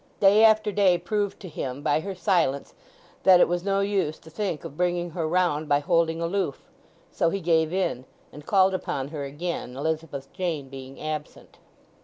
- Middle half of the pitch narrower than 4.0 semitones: No, average, 4.3 semitones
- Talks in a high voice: No, medium, 170 Hz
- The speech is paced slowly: No, average, 180 wpm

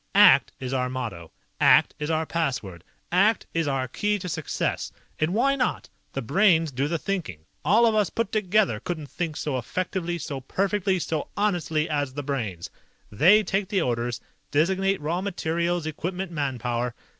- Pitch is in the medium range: Yes, medium, 160 Hz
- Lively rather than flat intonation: Yes, wide, 6.1 semitones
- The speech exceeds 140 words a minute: Yes, average, 165 wpm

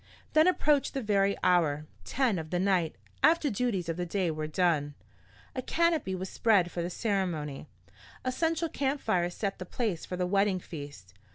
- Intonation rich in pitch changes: Yes, wide, 6.6 semitones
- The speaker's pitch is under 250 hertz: Yes, high, 190 Hz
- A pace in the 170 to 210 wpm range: Yes, average, 180 wpm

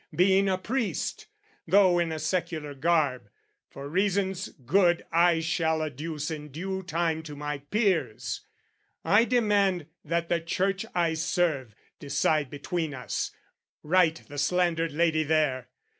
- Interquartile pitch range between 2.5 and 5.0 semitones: Yes, average, 3.6 semitones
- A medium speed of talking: No, slow, 130 wpm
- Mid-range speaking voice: Yes, medium, 165 Hz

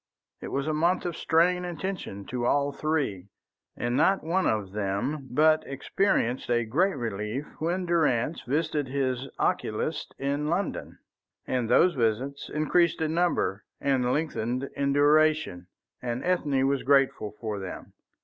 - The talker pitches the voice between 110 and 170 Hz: Yes, medium, 140 Hz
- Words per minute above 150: No, average, 145 wpm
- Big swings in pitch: No, average, 4.9 semitones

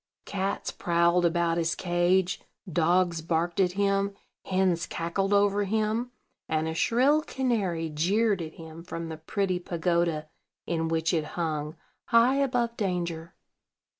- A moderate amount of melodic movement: Yes, average, 3.3 semitones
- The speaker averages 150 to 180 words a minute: No, slow, 135 wpm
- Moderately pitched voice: Yes, medium, 175 Hz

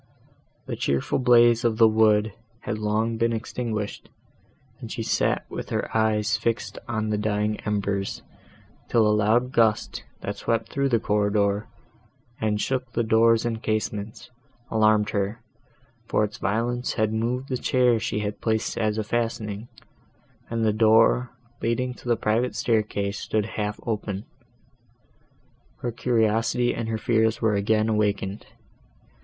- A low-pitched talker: Yes, low, 110 Hz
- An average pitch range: No, narrow, 1.7 semitones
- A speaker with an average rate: Yes, average, 145 wpm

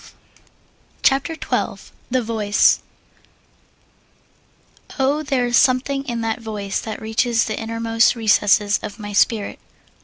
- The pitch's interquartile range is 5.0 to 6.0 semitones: No, average, 2.8 semitones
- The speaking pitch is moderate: No, high, 230 Hz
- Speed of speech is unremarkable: No, slow, 120 wpm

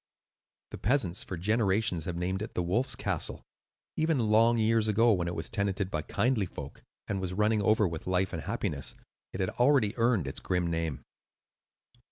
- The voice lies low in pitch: Yes, low, 100 Hz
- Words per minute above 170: Yes, average, 180 wpm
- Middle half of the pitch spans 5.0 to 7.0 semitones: No, average, 4.1 semitones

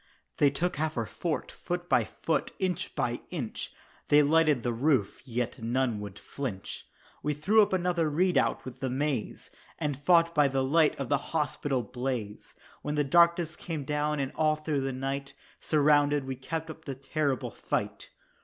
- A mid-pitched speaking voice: Yes, medium, 145 Hz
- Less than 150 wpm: No, average, 175 wpm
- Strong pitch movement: No, average, 3.3 semitones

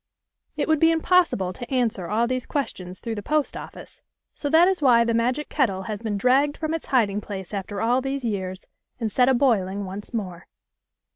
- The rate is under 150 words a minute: No, fast, 205 wpm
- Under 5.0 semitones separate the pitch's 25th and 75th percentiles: No, wide, 5.6 semitones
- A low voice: No, high, 235 Hz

